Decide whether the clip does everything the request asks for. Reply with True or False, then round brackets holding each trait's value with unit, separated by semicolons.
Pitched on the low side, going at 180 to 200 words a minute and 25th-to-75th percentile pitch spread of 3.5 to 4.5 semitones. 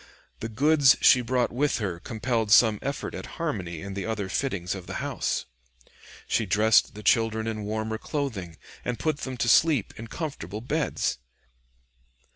False (110 Hz; 160 wpm; 4.2 semitones)